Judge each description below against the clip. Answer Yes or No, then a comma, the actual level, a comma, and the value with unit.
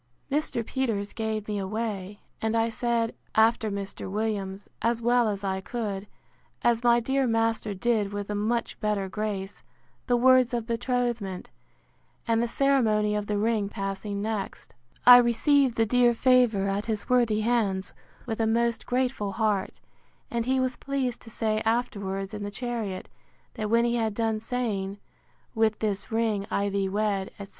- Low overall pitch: No, high, 220 Hz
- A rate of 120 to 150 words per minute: No, average, 165 wpm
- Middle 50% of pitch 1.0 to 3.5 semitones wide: Yes, average, 2.8 semitones